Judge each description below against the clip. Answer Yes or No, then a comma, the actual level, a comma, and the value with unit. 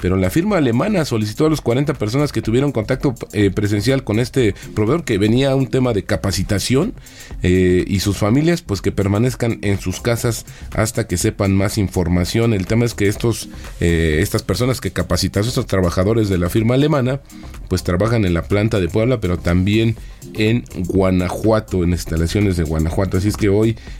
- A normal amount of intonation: Yes, average, 4.2 semitones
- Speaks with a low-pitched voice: Yes, low, 105 Hz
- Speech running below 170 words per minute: No, average, 185 wpm